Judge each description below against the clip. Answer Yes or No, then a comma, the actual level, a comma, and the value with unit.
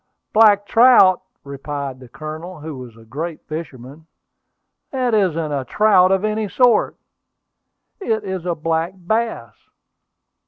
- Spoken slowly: Yes, slow, 125 wpm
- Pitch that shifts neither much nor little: No, wide, 6.4 semitones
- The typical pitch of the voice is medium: Yes, medium, 170 Hz